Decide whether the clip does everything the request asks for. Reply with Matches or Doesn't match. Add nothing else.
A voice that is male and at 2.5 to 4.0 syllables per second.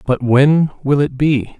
Matches